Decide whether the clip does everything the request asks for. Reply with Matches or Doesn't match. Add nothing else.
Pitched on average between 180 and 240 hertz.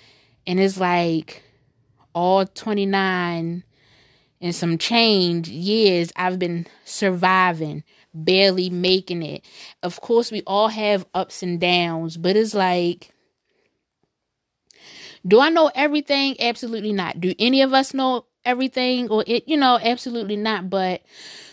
Matches